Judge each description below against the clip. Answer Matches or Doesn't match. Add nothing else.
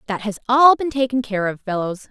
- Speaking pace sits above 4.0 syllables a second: Matches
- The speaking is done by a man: Doesn't match